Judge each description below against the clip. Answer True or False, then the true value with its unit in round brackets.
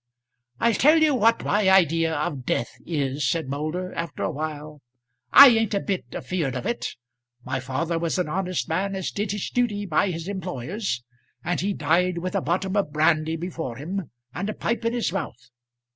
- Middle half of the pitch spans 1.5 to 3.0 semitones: False (4.5 semitones)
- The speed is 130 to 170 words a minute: False (190 wpm)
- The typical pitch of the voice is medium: True (175 Hz)